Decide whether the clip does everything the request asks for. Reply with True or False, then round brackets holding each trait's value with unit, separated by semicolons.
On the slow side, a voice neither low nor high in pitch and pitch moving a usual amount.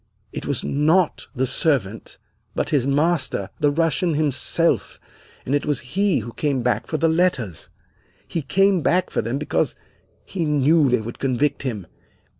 False (160 wpm; 145 Hz; 4.7 semitones)